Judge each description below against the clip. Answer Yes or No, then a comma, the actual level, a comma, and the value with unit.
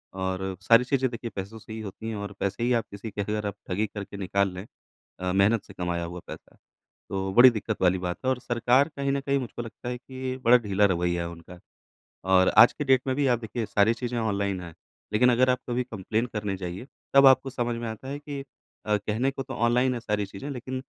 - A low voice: Yes, low, 110 Hz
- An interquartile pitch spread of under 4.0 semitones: No, average, 4.3 semitones